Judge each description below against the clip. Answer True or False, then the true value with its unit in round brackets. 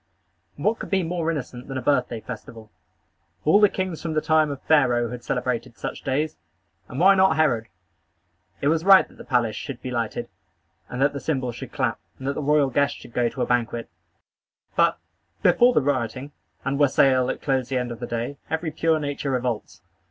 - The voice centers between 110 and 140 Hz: True (135 Hz)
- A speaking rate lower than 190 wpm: False (200 wpm)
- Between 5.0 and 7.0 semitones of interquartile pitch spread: False (4.2 semitones)